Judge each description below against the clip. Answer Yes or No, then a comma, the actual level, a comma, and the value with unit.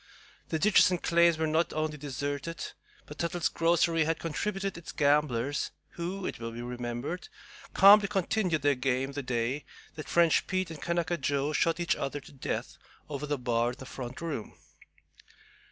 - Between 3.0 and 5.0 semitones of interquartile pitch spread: Yes, average, 4.1 semitones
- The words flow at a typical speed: Yes, average, 170 wpm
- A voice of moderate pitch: Yes, medium, 155 Hz